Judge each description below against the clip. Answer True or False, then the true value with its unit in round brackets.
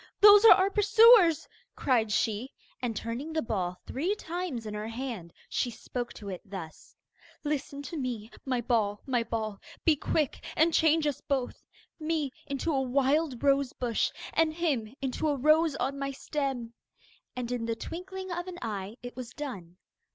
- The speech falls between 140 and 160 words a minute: False (170 wpm)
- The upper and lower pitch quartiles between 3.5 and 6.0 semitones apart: True (5.6 semitones)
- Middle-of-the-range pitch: False (265 Hz)